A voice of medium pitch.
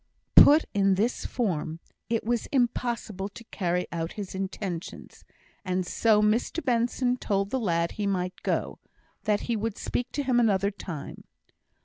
No: high, 205 Hz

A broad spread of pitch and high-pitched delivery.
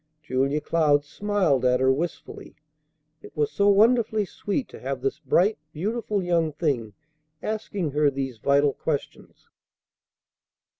No: wide, 6.7 semitones; medium, 150 Hz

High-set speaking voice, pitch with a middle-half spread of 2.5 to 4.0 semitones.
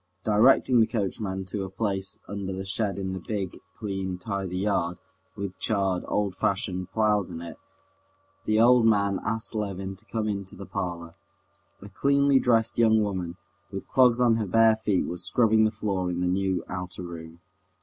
No: low, 100 Hz; average, 2.9 semitones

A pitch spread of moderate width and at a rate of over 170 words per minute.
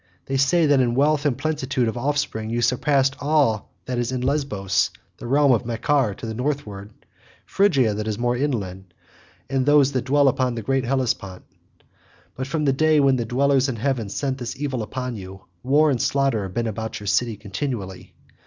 Yes: average, 4.0 semitones; average, 190 wpm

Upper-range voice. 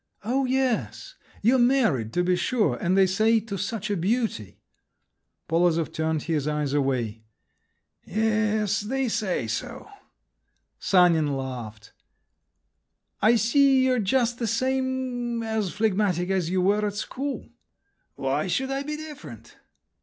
Yes: high, 210 Hz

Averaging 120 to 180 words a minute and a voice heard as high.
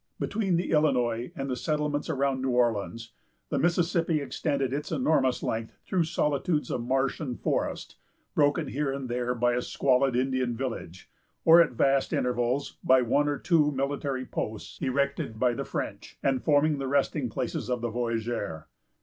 No: average, 165 wpm; low, 135 Hz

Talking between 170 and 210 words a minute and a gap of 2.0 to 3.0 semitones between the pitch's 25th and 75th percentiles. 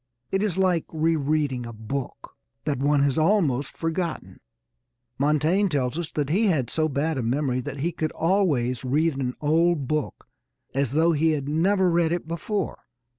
No: average, 175 wpm; average, 3.5 semitones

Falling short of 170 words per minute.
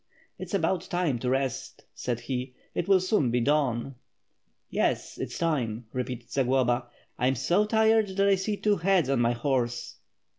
No: average, 175 wpm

